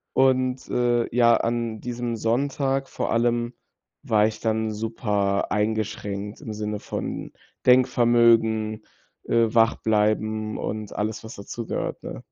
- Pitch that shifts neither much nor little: No, narrow, 1.9 semitones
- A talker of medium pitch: No, low, 115 Hz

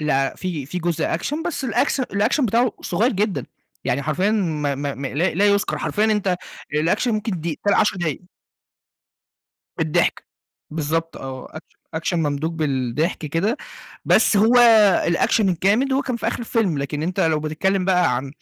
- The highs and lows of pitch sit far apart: Yes, wide, 5.7 semitones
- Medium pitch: Yes, medium, 175 Hz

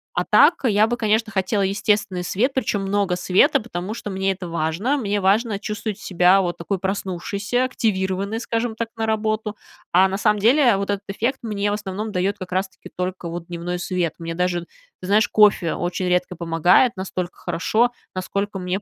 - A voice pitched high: Yes, high, 195 Hz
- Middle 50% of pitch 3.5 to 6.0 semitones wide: No, average, 3.1 semitones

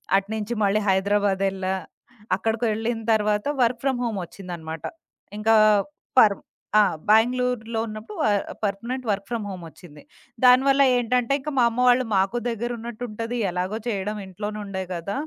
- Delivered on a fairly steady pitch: No, average, 3.5 semitones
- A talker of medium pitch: No, high, 215 Hz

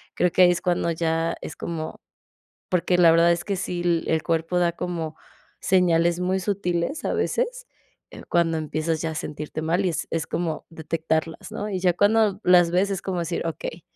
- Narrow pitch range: Yes, narrow, 2.0 semitones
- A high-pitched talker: No, medium, 170 Hz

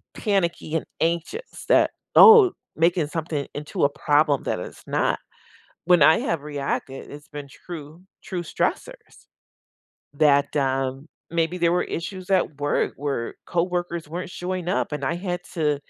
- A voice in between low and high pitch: Yes, medium, 160 Hz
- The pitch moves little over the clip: No, average, 3.5 semitones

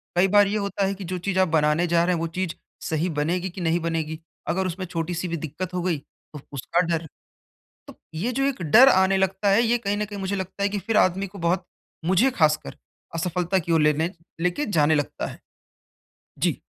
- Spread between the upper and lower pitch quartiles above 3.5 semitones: No, average, 3.1 semitones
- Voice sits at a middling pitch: Yes, medium, 180 Hz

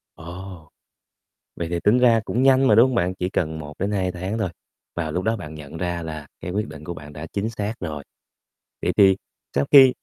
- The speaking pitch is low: Yes, very low, 90 Hz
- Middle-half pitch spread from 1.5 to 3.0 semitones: No, average, 5.0 semitones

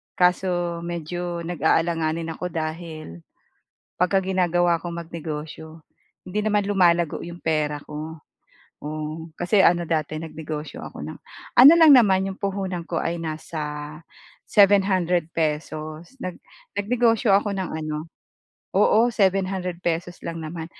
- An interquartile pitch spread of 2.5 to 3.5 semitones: Yes, average, 3.1 semitones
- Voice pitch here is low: No, medium, 170 Hz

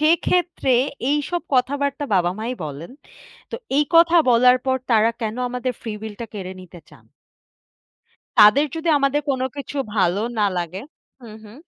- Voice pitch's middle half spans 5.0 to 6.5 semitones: Yes, wide, 5.4 semitones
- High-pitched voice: Yes, very high, 250 Hz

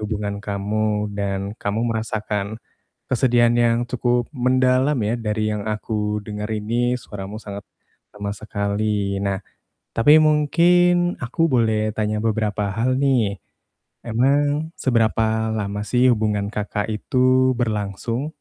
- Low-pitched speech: Yes, low, 110 Hz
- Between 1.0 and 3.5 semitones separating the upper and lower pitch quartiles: Yes, average, 3.0 semitones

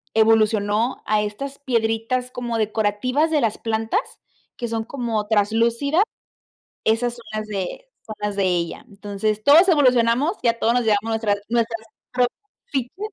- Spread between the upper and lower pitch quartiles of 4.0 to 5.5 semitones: No, average, 2.7 semitones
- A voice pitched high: Yes, high, 225 Hz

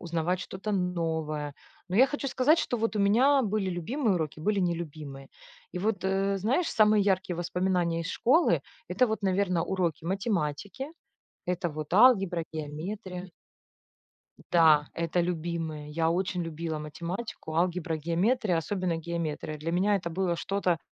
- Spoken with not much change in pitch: No, average, 3.4 semitones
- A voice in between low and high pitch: Yes, medium, 180 Hz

